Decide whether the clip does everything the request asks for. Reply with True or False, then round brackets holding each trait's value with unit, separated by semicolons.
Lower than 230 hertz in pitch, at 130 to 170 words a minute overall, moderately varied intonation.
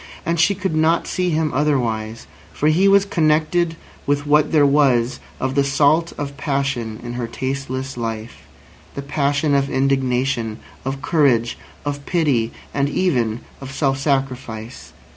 True (140 Hz; 140 wpm; 3.4 semitones)